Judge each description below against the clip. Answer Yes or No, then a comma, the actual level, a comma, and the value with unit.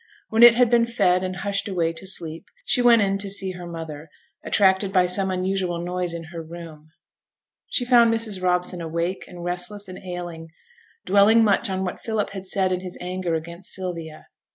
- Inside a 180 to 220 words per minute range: Yes, average, 190 wpm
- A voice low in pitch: No, medium, 185 Hz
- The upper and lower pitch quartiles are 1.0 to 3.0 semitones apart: Yes, narrow, 2.6 semitones